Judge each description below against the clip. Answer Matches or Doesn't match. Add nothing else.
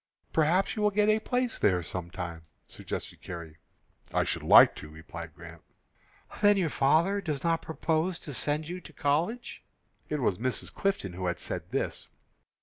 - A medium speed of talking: Matches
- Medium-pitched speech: Matches